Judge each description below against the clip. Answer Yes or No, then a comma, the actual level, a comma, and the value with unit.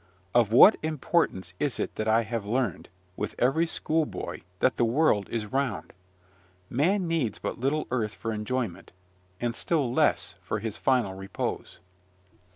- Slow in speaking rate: No, average, 150 wpm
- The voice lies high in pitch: No, low, 120 Hz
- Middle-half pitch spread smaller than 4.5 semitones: No, average, 5.2 semitones